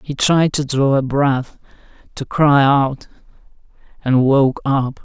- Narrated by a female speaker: No, male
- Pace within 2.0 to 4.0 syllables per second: Yes, 3.6 syllables/s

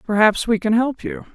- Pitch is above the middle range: Yes, high, 230 Hz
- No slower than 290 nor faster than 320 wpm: No, fast, 225 wpm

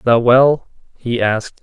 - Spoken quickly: No, average, 150 wpm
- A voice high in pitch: No, low, 120 Hz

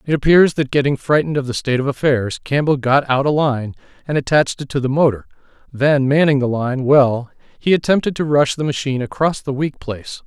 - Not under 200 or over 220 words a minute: Yes, fast, 205 wpm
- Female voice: No, male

